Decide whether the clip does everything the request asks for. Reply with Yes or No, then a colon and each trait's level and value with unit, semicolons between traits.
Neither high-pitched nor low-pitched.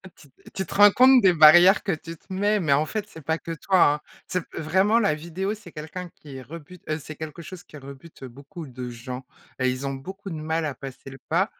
Yes: medium, 160 Hz